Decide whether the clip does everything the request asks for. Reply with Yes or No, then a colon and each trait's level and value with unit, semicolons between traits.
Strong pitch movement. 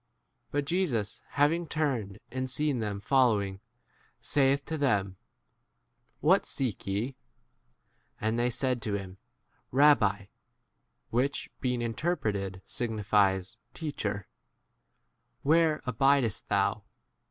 Yes: wide, 5.8 semitones